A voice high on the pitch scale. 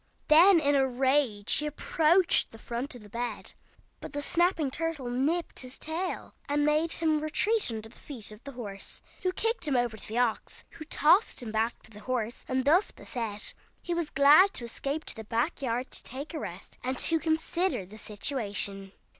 Yes: very high, 275 Hz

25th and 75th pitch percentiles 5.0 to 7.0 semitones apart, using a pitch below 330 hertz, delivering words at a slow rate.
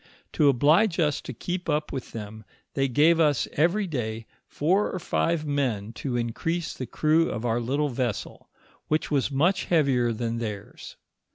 No: wide, 5.5 semitones; medium, 140 Hz; average, 165 wpm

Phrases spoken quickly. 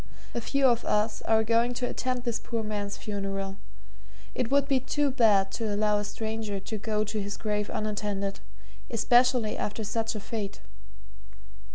No: average, 165 wpm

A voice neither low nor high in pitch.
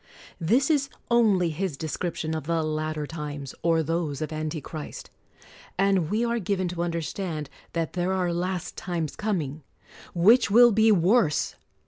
Yes: medium, 170 Hz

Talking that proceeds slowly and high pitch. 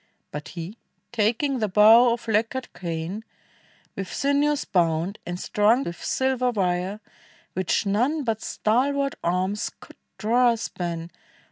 Yes: slow, 130 wpm; high, 215 Hz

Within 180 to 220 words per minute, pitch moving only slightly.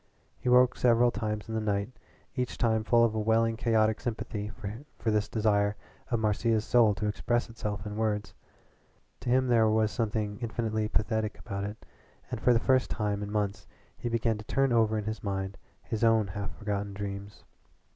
Yes: average, 185 wpm; narrow, 2.0 semitones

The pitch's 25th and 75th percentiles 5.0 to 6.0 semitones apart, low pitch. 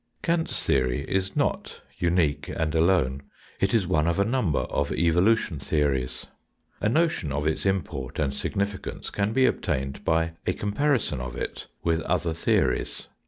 Yes: wide, 5.4 semitones; very low, 85 Hz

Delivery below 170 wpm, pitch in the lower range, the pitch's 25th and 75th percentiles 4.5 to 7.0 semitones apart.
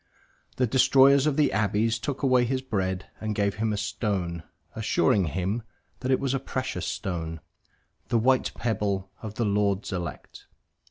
Yes: average, 160 wpm; low, 110 Hz; average, 4.8 semitones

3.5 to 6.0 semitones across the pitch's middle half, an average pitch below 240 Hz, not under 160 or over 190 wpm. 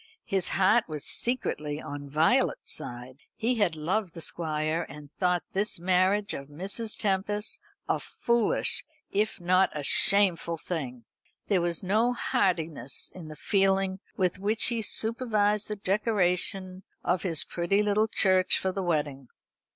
No: average, 4.3 semitones; medium, 185 Hz; average, 145 wpm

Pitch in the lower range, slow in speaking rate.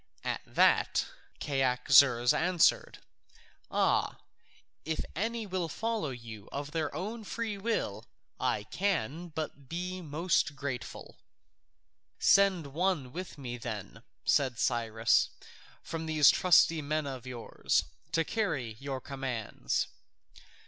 No: medium, 150 Hz; slow, 115 wpm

